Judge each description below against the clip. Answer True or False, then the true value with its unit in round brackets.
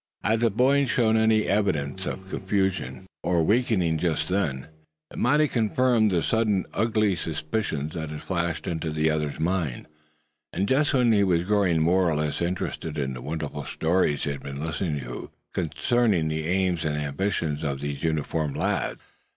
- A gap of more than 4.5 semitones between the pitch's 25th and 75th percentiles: True (5.3 semitones)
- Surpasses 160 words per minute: True (170 wpm)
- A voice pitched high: False (85 Hz)